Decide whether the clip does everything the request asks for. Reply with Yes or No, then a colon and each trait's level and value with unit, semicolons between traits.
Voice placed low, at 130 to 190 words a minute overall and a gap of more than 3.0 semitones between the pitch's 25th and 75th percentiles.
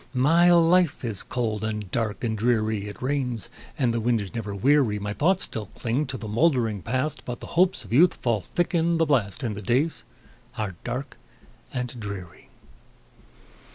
Yes: low, 120 Hz; average, 180 wpm; average, 5.3 semitones